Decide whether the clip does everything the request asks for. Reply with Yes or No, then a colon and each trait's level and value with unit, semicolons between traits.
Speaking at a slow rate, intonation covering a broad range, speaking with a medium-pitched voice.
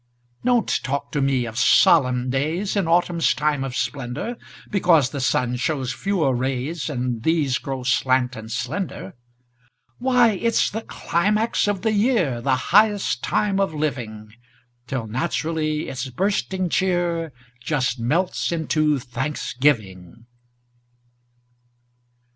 Yes: slow, 120 wpm; wide, 6.1 semitones; medium, 145 Hz